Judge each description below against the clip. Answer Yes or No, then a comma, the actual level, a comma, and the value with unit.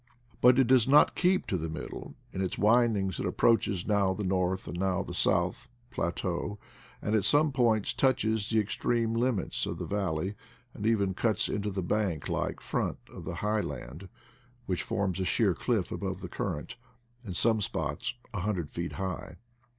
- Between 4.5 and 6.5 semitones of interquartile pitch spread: No, average, 3.4 semitones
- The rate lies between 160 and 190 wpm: Yes, average, 175 wpm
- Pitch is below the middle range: Yes, low, 100 Hz